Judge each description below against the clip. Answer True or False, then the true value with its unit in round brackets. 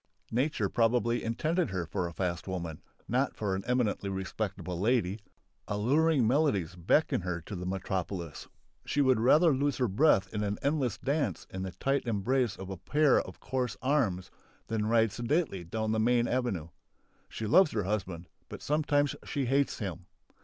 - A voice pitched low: True (110 Hz)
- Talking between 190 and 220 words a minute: False (165 wpm)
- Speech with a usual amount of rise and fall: False (5.9 semitones)